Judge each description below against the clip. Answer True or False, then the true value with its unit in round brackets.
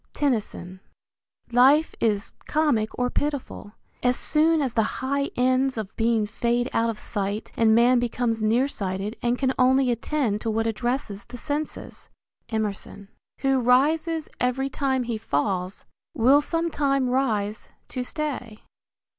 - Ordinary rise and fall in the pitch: True (3.8 semitones)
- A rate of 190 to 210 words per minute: False (140 wpm)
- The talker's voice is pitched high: True (245 Hz)